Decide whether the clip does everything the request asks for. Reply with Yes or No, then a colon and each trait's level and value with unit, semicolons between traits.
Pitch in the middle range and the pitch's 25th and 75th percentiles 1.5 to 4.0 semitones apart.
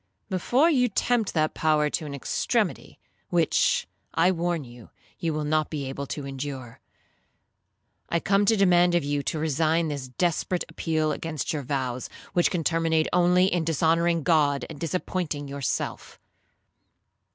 Yes: medium, 160 Hz; average, 3.4 semitones